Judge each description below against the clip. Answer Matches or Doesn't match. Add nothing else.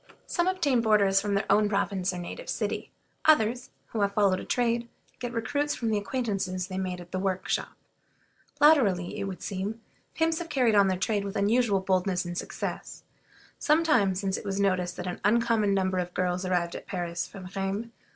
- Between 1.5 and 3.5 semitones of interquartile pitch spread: Doesn't match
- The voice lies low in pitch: Doesn't match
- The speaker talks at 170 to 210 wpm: Matches